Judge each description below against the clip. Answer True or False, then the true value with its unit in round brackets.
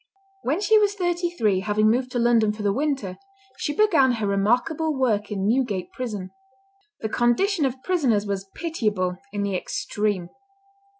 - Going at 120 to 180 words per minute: True (160 wpm)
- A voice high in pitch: True (235 Hz)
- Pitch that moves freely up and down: True (6.4 semitones)